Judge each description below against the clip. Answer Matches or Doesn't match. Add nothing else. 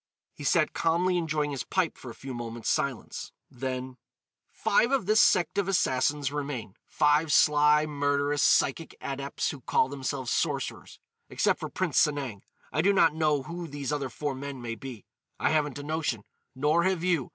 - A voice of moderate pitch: Matches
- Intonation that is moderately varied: Matches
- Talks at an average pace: Matches